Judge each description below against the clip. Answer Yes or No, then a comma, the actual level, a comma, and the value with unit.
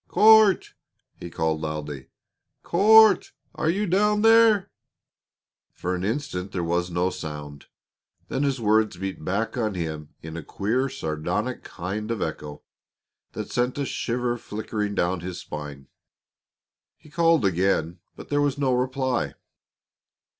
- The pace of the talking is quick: No, average, 140 wpm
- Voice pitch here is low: Yes, low, 105 Hz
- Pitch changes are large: Yes, wide, 8.5 semitones